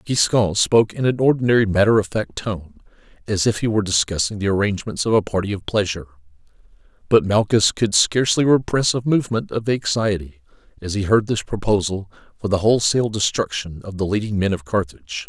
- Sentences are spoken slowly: No, average, 175 wpm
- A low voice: Yes, low, 100 Hz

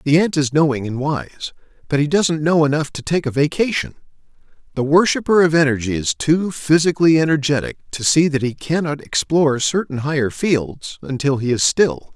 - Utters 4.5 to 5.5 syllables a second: Yes, 5.4 syllables/s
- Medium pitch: Yes, medium, 150 Hz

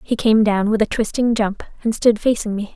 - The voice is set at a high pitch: Yes, high, 215 Hz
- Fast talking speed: Yes, fast, 240 wpm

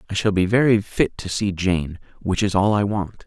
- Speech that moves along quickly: Yes, fast, 220 wpm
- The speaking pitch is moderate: No, low, 100 Hz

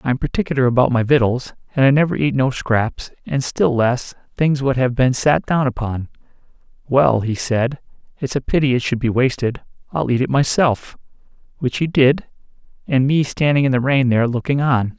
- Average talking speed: Yes, average, 190 wpm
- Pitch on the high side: No, low, 130 Hz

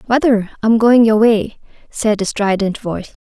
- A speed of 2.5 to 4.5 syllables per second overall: No, 4.7 syllables/s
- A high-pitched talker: Yes, high, 220 Hz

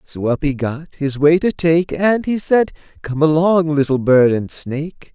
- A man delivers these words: Yes, male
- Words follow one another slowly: No, average, 200 wpm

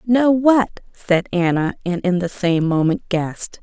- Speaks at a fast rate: No, average, 165 wpm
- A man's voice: No, female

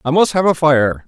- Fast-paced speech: Yes, fast, 280 wpm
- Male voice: Yes, male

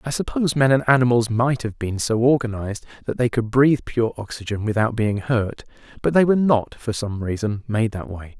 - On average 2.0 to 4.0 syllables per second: No, 5.5 syllables/s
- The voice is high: No, low, 120 Hz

